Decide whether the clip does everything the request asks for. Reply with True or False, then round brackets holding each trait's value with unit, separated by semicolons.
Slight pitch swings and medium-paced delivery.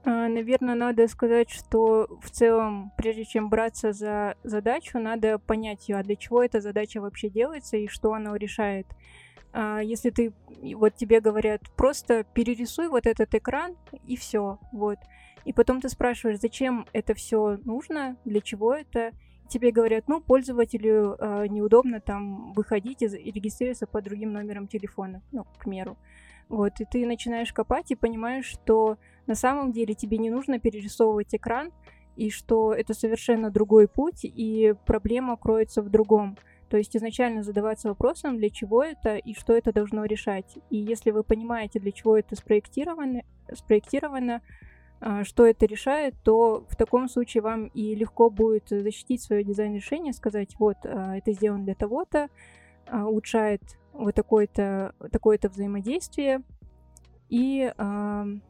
True (2.2 semitones; 145 wpm)